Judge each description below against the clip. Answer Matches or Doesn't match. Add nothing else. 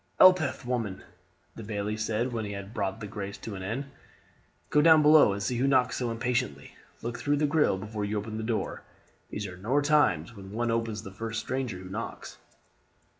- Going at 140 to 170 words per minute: Doesn't match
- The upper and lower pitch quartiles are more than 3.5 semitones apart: Matches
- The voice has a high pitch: Doesn't match